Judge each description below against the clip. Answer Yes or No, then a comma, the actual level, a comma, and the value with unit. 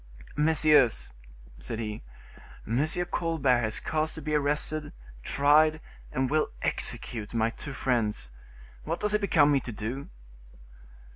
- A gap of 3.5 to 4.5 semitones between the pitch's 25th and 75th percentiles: No, average, 4.9 semitones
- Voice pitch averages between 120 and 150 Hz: Yes, medium, 140 Hz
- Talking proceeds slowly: Yes, slow, 130 wpm